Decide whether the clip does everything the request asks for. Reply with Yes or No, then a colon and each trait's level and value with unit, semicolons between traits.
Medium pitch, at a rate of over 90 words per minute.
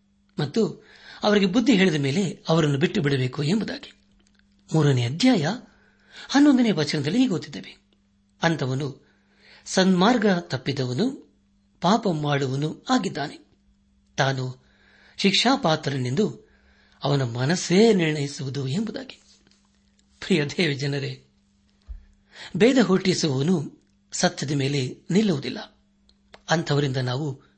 No: medium, 150 Hz; average, 80 wpm